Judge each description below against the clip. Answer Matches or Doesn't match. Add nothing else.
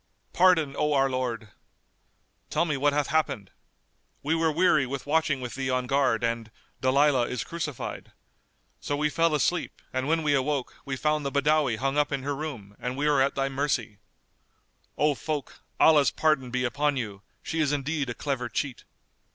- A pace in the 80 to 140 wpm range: Doesn't match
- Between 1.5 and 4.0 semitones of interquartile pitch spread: Matches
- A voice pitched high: Doesn't match